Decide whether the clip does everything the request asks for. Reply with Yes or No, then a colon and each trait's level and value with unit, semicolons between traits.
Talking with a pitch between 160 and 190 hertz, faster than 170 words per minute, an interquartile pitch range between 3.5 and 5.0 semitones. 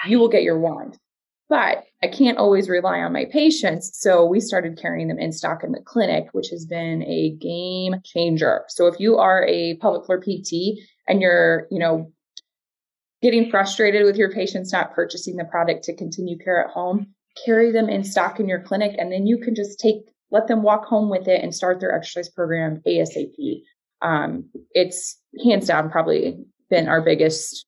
Yes: medium, 185 Hz; average, 190 wpm; average, 3.9 semitones